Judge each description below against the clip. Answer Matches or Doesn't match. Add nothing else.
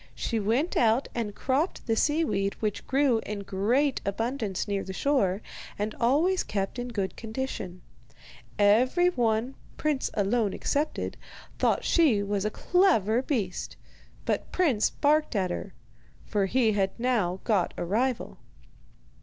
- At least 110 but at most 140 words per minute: Matches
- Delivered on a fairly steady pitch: Doesn't match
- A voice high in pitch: Matches